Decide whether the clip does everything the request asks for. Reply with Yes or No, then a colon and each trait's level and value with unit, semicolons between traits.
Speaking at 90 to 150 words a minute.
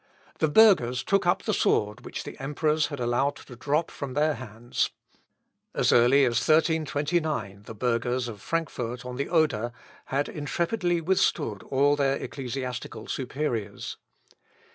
Yes: average, 140 wpm